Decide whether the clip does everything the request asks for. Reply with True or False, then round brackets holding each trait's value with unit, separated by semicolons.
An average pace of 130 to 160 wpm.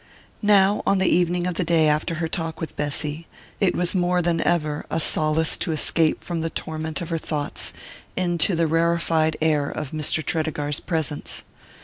False (175 wpm)